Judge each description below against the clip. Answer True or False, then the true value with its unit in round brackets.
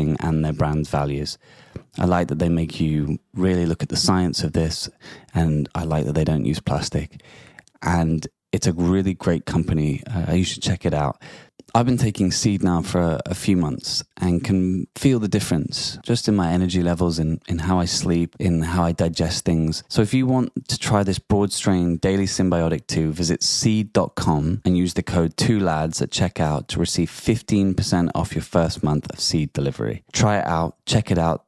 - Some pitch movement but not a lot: True (3.0 semitones)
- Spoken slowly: False (200 wpm)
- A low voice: True (90 Hz)